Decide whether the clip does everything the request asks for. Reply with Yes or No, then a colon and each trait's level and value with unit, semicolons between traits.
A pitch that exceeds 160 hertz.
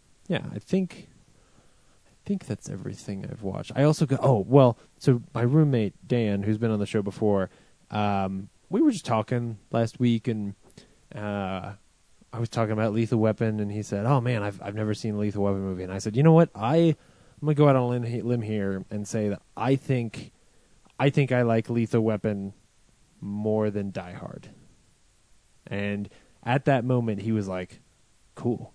No: low, 110 Hz